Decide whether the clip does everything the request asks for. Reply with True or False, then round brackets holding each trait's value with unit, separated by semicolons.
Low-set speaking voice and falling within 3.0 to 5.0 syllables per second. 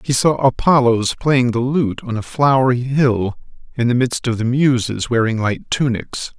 True (125 Hz; 4.5 syllables/s)